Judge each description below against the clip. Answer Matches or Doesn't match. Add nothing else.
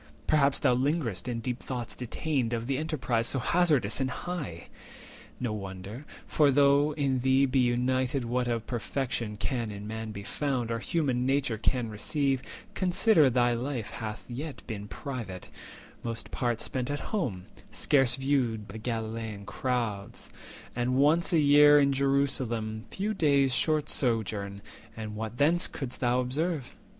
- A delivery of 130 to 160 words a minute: Matches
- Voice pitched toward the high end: Doesn't match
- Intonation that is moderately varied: Matches